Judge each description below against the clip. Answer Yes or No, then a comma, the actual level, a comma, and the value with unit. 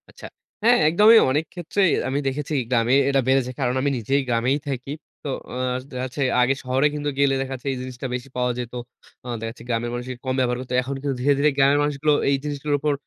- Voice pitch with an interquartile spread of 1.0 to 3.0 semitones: Yes, narrow, 2.5 semitones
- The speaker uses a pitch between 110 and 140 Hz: Yes, low, 135 Hz